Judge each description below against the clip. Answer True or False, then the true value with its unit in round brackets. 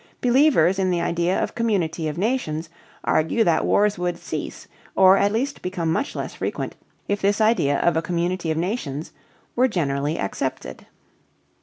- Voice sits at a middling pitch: True (180 Hz)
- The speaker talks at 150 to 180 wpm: True (165 wpm)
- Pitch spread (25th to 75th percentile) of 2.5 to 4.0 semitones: False (4.6 semitones)